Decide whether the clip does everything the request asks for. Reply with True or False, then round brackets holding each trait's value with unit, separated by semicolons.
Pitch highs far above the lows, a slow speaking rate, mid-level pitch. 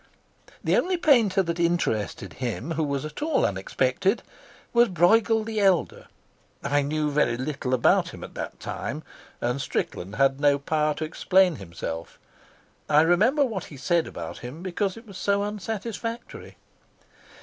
False (6.8 semitones; 150 wpm; 165 Hz)